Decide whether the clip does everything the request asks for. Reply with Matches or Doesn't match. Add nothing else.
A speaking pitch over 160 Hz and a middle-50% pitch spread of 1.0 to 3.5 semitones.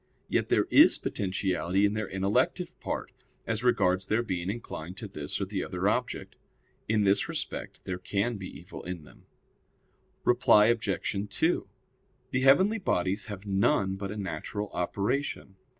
Doesn't match